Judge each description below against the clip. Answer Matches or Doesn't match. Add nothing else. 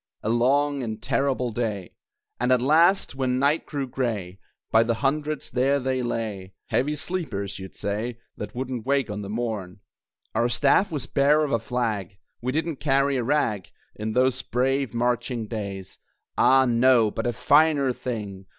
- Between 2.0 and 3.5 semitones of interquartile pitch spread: Doesn't match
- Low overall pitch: Matches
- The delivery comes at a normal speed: Matches